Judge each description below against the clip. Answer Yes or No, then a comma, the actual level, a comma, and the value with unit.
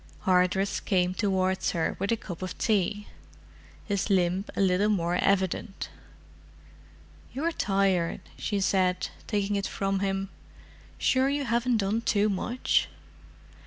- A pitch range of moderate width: No, narrow, 2.2 semitones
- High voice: Yes, high, 195 Hz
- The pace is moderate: No, slow, 125 wpm